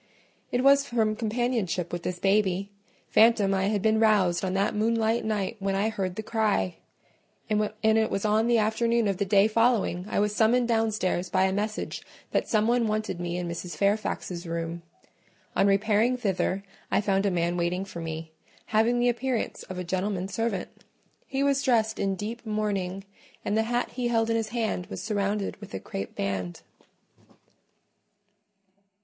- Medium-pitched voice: No, high, 210 Hz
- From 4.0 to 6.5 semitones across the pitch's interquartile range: No, average, 3.2 semitones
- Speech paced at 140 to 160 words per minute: No, average, 175 wpm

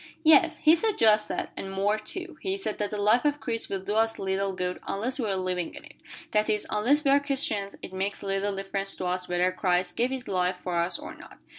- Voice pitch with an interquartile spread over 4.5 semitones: Yes, average, 4.9 semitones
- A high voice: Yes, high, 205 Hz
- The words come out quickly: Yes, fast, 245 wpm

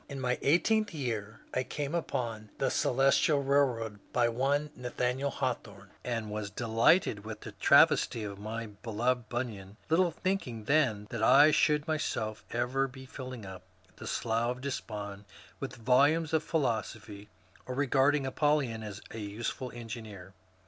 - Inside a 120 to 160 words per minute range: Yes, average, 150 wpm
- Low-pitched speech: Yes, low, 120 Hz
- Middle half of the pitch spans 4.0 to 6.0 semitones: Yes, average, 4.4 semitones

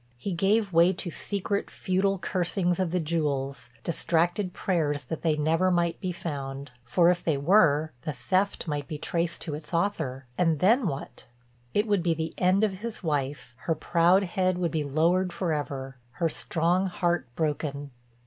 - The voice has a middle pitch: Yes, medium, 170 Hz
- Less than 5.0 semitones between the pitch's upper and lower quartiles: Yes, average, 3.8 semitones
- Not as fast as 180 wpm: Yes, average, 170 wpm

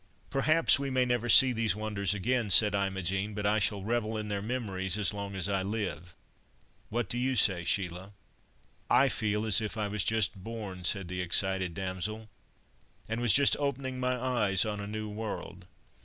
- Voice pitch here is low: Yes, low, 105 Hz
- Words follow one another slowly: No, average, 185 wpm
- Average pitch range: Yes, average, 3.3 semitones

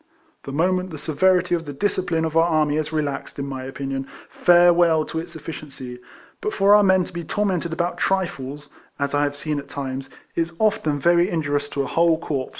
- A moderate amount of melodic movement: Yes, average, 3.5 semitones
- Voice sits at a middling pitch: Yes, medium, 160 Hz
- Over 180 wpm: Yes, average, 200 wpm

